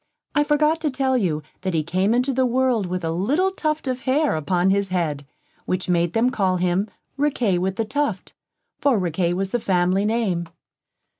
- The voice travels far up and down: Yes, wide, 6.4 semitones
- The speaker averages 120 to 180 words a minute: No, average, 190 wpm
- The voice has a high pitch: Yes, high, 200 Hz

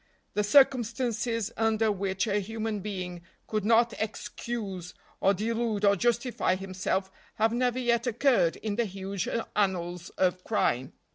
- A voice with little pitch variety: No, average, 3.4 semitones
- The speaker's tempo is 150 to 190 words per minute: No, slow, 135 wpm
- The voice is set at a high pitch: Yes, high, 210 Hz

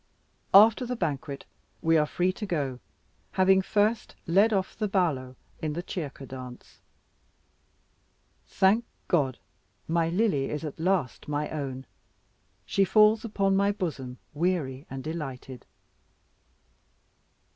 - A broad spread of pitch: Yes, wide, 6.1 semitones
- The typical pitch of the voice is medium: Yes, medium, 165 Hz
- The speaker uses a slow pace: Yes, slow, 120 wpm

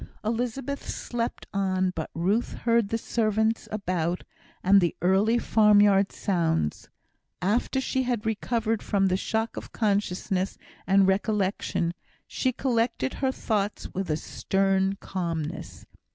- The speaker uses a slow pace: Yes, slow, 125 wpm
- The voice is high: Yes, high, 200 Hz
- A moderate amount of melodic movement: Yes, average, 3.3 semitones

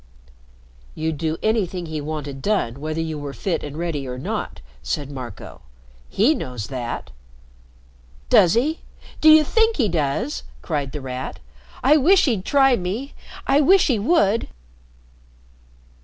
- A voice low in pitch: No, medium, 170 Hz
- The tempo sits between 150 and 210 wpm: No, average, 140 wpm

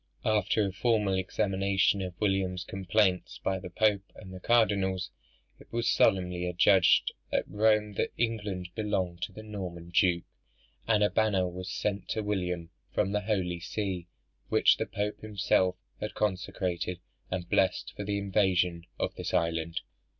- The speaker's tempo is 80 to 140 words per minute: No, average, 150 wpm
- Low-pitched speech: Yes, very low, 95 Hz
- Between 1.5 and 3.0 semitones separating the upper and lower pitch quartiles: Yes, narrow, 2.5 semitones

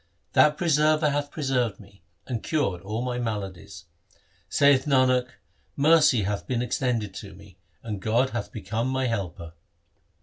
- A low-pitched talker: Yes, low, 120 Hz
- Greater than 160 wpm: No, average, 140 wpm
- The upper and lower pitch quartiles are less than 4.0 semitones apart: No, average, 5.2 semitones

